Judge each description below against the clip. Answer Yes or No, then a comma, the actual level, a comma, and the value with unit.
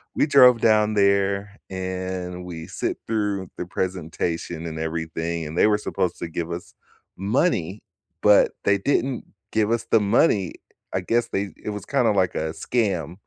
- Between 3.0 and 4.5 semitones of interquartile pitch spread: Yes, average, 3.7 semitones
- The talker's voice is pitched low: Yes, very low, 95 Hz